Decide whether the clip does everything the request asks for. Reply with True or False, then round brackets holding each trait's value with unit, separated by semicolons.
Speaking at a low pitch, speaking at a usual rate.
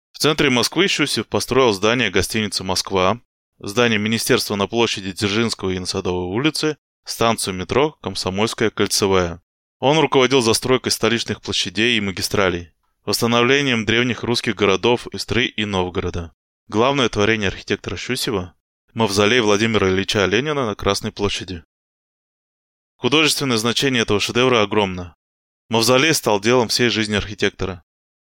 True (105 Hz; 120 wpm)